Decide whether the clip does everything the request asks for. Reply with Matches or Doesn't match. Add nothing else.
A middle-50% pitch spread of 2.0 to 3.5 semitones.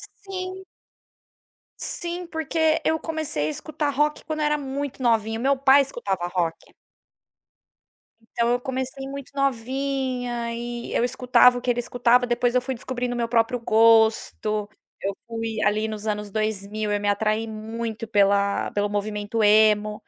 Doesn't match